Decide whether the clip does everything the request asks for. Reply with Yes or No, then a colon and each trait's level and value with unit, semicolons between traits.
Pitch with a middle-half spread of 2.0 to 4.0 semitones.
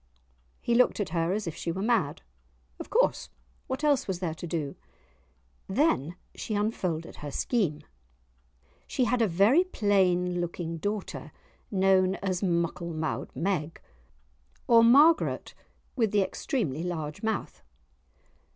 No: average, 5.1 semitones